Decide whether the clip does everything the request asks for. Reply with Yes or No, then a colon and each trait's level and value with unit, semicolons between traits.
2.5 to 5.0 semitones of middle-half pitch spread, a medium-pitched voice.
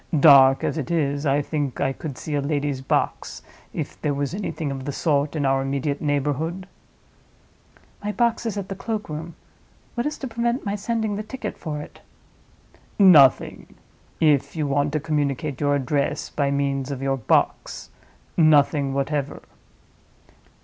Yes: average, 3.5 semitones; medium, 145 Hz